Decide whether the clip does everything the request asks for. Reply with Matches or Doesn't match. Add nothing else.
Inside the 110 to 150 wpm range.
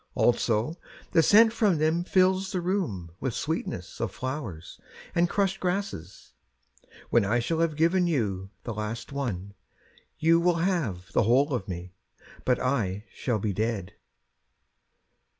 Matches